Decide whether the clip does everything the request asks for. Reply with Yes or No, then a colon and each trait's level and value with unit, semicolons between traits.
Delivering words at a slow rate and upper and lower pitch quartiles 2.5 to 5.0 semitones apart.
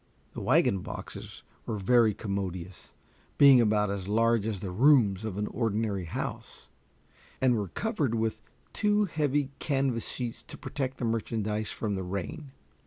No: average, 150 wpm; average, 4.5 semitones